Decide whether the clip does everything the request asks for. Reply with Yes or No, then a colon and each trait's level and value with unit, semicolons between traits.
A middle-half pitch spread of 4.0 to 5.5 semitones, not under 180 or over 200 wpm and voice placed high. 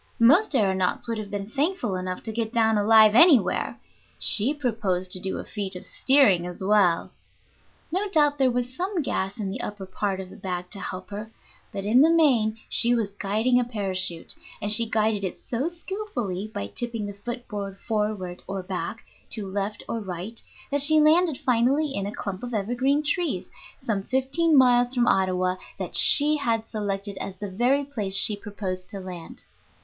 Yes: average, 4.7 semitones; average, 185 wpm; high, 215 Hz